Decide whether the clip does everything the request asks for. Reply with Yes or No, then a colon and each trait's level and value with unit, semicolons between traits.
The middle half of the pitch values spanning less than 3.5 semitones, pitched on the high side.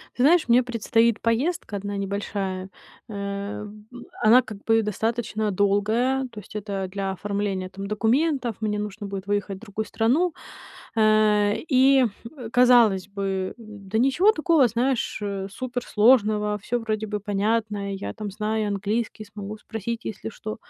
Yes: narrow, 2.6 semitones; high, 215 Hz